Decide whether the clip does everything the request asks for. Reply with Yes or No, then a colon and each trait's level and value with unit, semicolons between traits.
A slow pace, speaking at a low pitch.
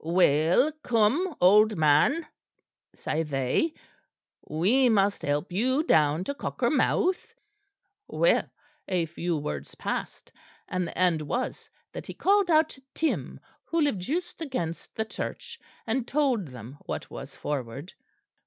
No: slow, 130 wpm; high, 200 Hz